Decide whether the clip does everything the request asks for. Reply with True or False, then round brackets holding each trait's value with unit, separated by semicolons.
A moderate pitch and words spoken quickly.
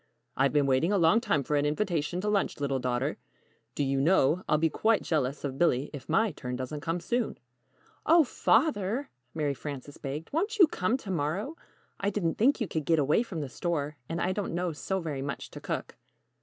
True (165 Hz; 210 wpm)